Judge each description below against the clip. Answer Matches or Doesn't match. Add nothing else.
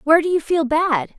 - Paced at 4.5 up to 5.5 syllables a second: Doesn't match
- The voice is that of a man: Doesn't match